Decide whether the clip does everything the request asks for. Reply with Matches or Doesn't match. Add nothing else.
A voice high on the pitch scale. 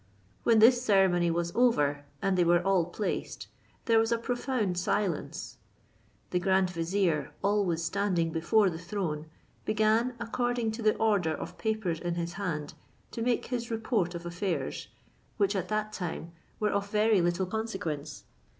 Matches